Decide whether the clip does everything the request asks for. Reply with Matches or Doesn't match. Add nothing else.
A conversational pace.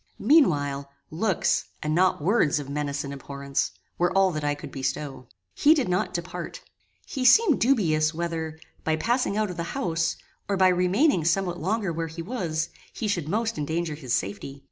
Matches